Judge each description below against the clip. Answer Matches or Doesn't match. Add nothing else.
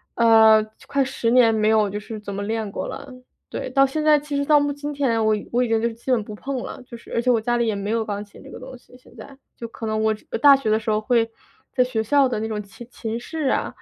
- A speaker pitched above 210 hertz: Matches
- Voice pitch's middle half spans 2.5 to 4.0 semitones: Matches